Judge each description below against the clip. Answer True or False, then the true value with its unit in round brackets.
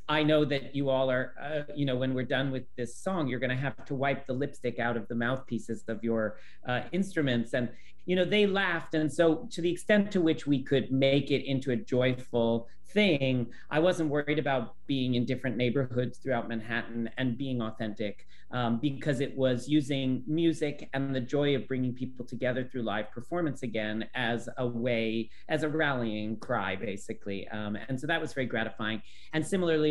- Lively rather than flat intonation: False (3.8 semitones)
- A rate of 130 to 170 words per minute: False (195 wpm)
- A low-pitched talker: True (130 Hz)